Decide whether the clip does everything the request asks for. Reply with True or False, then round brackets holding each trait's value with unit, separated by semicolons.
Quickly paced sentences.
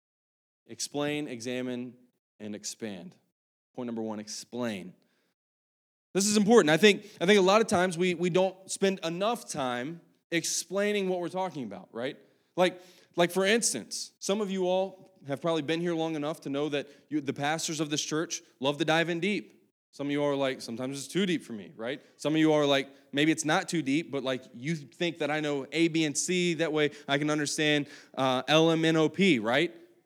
True (210 wpm)